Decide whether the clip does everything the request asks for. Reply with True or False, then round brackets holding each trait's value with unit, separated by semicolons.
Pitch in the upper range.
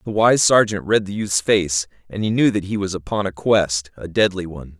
False (100 Hz)